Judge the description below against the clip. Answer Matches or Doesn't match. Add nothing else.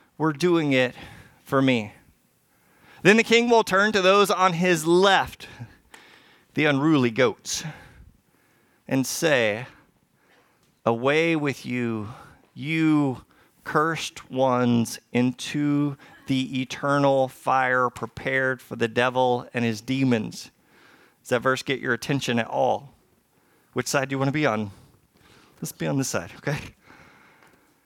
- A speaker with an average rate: Doesn't match